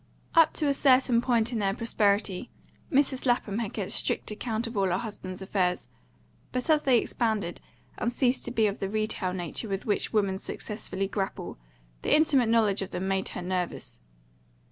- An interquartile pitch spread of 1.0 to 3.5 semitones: No, average, 4.0 semitones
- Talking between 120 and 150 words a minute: No, average, 180 wpm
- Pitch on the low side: No, high, 215 Hz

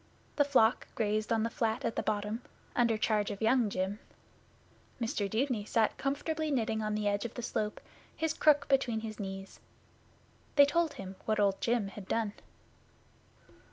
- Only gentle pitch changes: No, average, 3.4 semitones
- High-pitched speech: Yes, high, 220 Hz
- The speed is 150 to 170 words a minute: Yes, average, 165 wpm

